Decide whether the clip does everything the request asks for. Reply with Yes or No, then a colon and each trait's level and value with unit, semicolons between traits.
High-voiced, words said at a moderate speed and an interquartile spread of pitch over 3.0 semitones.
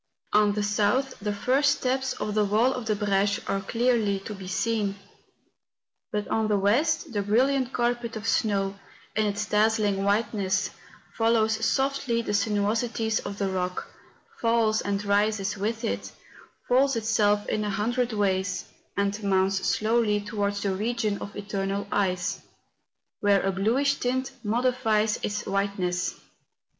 No: high, 210 Hz; average, 145 wpm; narrow, 2.5 semitones